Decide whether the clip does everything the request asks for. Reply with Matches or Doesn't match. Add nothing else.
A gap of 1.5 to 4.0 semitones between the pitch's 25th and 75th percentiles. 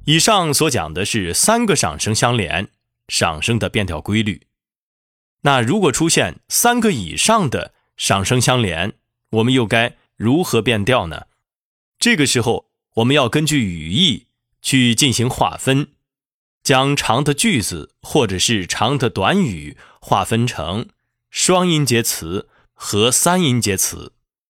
Doesn't match